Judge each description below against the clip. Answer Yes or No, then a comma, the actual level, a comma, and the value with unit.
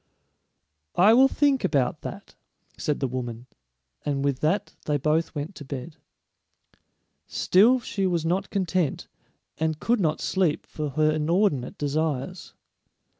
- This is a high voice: No, medium, 155 Hz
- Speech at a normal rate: No, slow, 130 wpm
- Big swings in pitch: No, average, 4.7 semitones